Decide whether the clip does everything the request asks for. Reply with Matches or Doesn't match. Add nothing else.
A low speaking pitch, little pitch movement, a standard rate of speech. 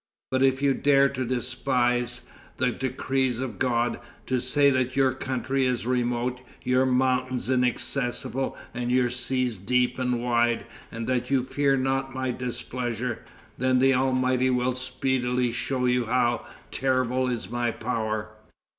Matches